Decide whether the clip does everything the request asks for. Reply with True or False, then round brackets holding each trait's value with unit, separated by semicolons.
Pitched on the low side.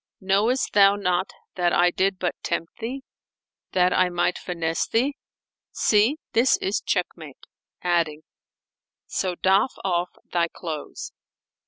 False (185 Hz)